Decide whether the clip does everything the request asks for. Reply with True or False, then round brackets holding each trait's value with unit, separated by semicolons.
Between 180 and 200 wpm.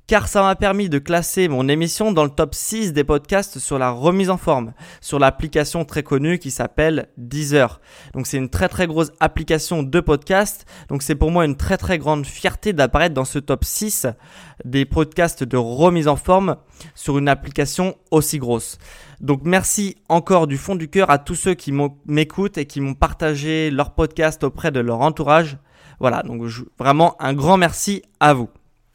True (185 wpm)